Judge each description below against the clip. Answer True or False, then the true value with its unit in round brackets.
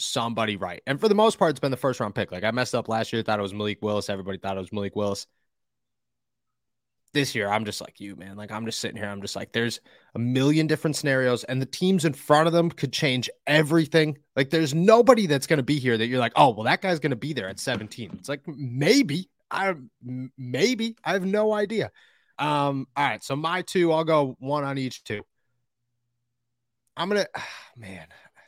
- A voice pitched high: False (130 Hz)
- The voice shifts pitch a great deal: True (6.0 semitones)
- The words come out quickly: True (220 wpm)